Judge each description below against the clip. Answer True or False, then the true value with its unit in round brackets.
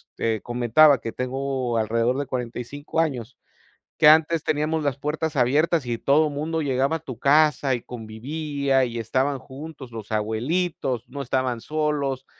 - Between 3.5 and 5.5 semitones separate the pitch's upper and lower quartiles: True (3.8 semitones)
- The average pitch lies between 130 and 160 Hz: True (135 Hz)